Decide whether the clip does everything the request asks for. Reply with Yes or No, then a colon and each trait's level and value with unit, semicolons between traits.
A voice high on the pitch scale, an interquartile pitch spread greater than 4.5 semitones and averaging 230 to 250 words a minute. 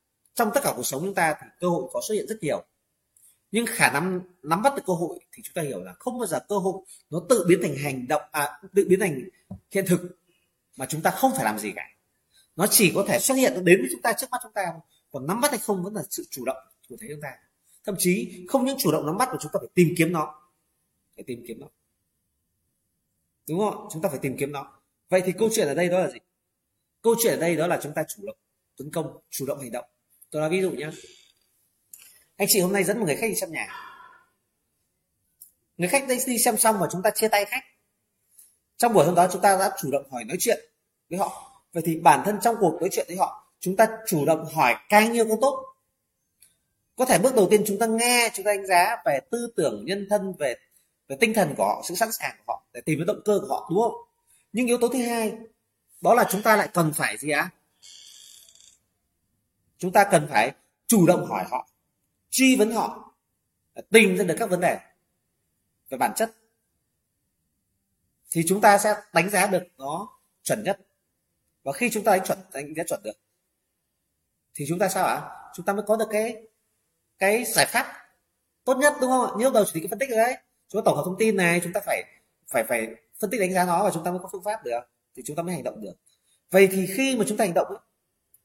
Yes: high, 195 Hz; average, 5.2 semitones; average, 240 wpm